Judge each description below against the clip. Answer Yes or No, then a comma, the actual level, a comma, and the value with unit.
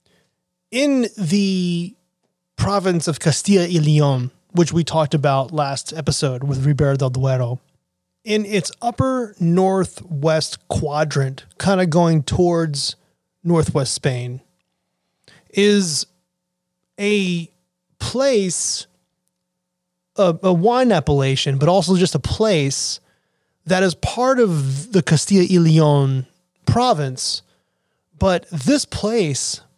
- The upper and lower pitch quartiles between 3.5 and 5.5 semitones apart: Yes, average, 5.0 semitones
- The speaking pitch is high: No, medium, 170 Hz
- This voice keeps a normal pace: No, slow, 105 wpm